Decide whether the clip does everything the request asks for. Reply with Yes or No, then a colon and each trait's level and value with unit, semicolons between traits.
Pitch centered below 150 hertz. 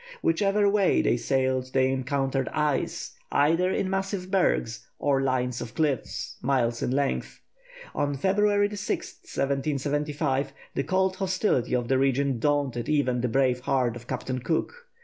Yes: medium, 140 Hz